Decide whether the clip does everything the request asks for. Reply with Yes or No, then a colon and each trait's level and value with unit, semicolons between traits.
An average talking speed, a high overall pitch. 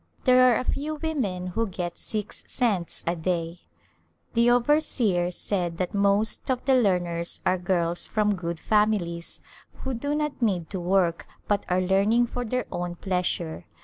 Yes: average, 160 wpm; high, 195 Hz